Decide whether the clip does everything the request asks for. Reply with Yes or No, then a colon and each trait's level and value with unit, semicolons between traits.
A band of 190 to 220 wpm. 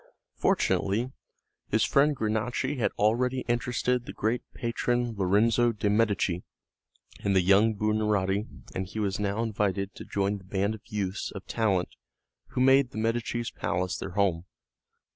No: average, 145 wpm